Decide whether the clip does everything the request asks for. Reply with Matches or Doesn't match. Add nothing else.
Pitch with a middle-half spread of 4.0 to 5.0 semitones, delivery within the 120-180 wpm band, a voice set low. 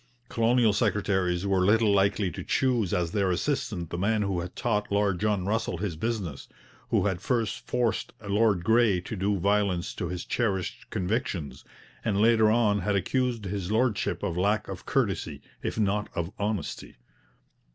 Doesn't match